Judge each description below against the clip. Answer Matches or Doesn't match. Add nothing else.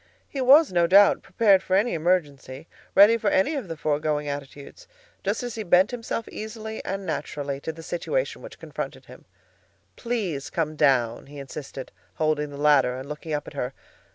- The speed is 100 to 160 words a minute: Doesn't match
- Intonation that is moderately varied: Doesn't match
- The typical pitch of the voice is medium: Matches